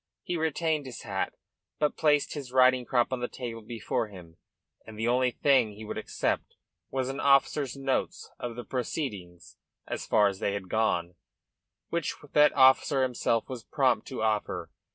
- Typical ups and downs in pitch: Yes, average, 3.9 semitones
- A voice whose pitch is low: Yes, low, 125 Hz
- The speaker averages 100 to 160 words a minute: No, average, 170 wpm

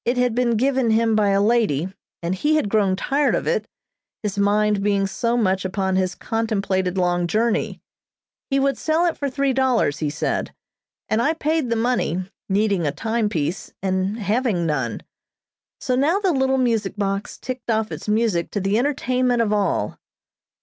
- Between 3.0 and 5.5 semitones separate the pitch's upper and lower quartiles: Yes, average, 4.6 semitones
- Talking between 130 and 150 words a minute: No, average, 175 wpm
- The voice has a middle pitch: No, high, 215 Hz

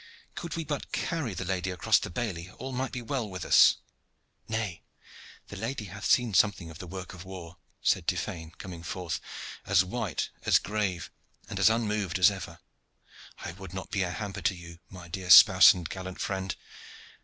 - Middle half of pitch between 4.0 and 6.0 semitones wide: No, average, 3.2 semitones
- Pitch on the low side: Yes, very low, 95 Hz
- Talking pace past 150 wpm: Yes, average, 185 wpm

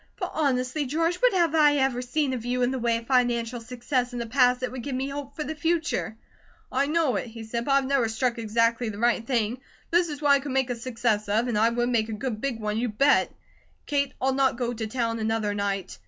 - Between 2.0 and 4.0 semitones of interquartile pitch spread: Yes, average, 3.3 semitones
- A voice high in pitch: Yes, very high, 250 Hz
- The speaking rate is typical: No, fast, 250 wpm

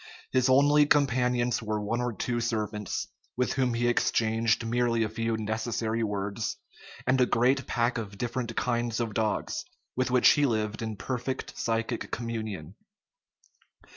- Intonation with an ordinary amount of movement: No, narrow, 2.0 semitones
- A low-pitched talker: Yes, low, 115 Hz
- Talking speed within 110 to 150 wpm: Yes, average, 145 wpm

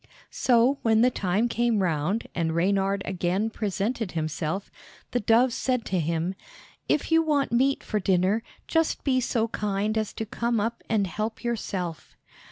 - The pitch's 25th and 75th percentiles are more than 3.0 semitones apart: Yes, average, 4.2 semitones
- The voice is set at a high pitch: Yes, high, 215 Hz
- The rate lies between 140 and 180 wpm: Yes, average, 160 wpm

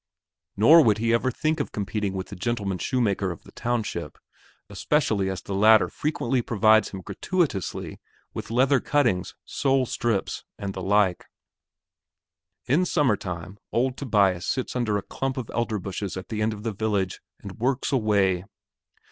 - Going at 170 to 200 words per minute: No, average, 155 wpm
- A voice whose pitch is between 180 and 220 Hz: No, low, 110 Hz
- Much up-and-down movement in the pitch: No, average, 4.5 semitones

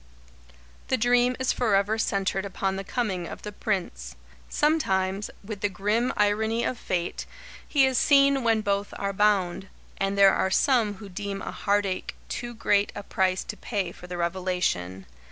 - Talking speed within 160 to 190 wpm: Yes, average, 165 wpm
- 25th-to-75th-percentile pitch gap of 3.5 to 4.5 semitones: No, average, 3.1 semitones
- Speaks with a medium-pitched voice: No, high, 200 Hz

